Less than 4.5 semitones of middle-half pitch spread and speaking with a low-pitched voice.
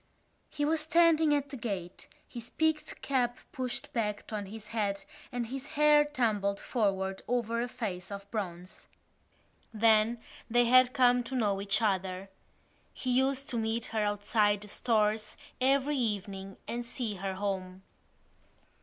No: average, 4.1 semitones; high, 225 Hz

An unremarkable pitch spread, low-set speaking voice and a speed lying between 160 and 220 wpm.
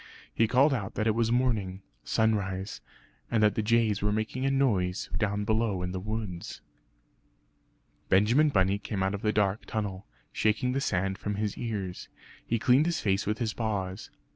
Yes: average, 3.0 semitones; low, 105 Hz; average, 175 wpm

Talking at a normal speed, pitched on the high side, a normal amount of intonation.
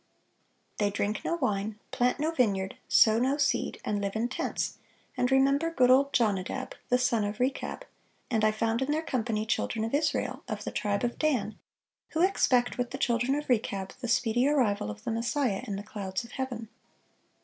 Yes: average, 190 wpm; high, 240 Hz; average, 4.0 semitones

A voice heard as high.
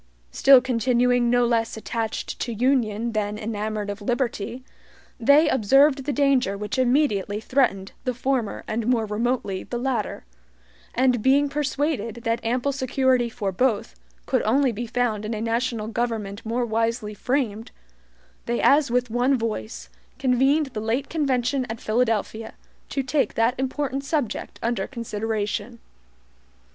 Yes: high, 240 Hz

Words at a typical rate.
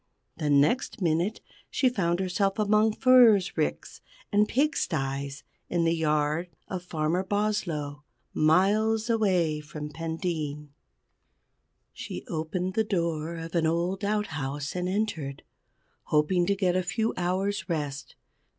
No: slow, 125 wpm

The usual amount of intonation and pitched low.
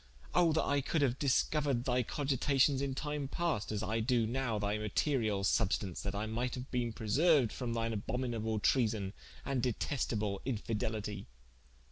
Yes: average, 4.2 semitones; low, 120 Hz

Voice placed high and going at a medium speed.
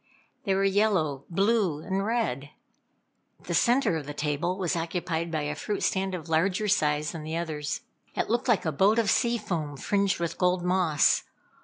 No: medium, 180 Hz; average, 180 wpm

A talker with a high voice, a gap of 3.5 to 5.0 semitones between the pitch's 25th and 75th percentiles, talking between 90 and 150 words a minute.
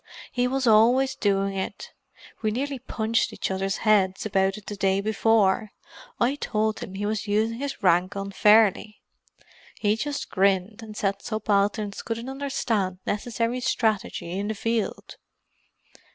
No: high, 215 Hz; average, 2.7 semitones; average, 140 wpm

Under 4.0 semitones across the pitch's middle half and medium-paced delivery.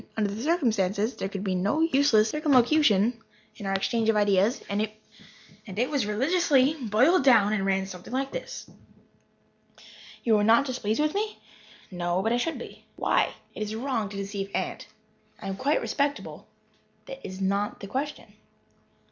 No: wide, 5.6 semitones; average, 160 wpm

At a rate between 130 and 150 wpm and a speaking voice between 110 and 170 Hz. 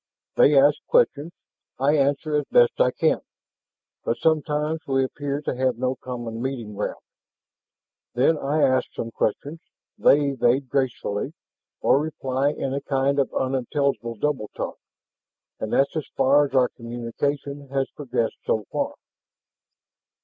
Yes: average, 140 wpm; low, 135 Hz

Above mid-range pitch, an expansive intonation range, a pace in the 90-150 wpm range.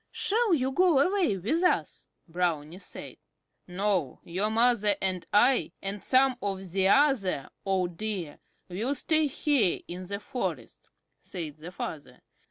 Yes: high, 200 Hz; wide, 6.8 semitones; average, 140 wpm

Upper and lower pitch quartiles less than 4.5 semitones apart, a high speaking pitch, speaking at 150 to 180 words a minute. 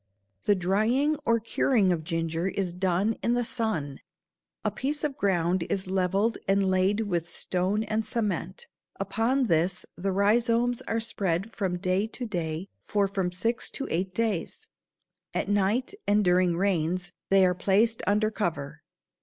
Yes: average, 3.9 semitones; high, 195 Hz; average, 155 wpm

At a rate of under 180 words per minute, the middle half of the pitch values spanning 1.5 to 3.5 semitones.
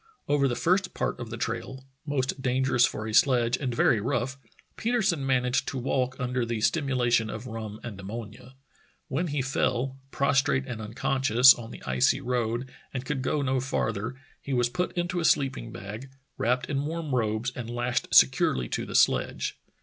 No: average, 185 wpm; narrow, 2.6 semitones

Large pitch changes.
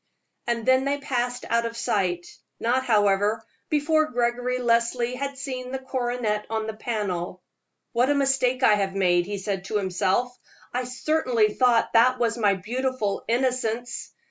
No: average, 3.3 semitones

